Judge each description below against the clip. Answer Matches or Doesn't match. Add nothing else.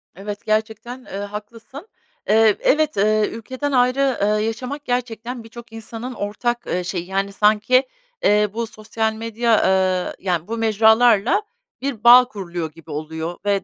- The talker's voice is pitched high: Matches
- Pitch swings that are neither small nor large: Matches